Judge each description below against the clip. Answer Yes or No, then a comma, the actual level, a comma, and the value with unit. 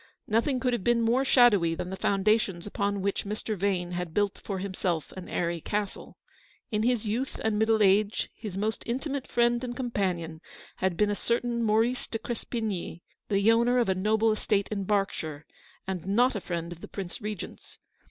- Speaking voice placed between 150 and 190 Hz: No, high, 210 Hz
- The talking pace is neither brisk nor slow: Yes, average, 185 wpm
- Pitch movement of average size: Yes, average, 3.6 semitones